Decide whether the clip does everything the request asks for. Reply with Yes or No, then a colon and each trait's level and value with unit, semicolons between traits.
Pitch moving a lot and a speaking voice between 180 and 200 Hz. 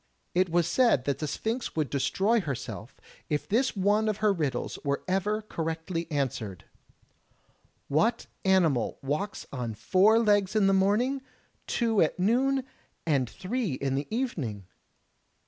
Yes: wide, 7.3 semitones; medium, 185 Hz